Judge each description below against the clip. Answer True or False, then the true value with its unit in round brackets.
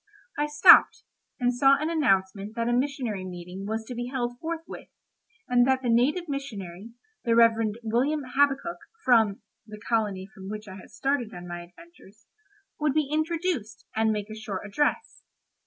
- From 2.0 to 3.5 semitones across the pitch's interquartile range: False (5.2 semitones)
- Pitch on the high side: True (235 Hz)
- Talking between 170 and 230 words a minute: False (160 wpm)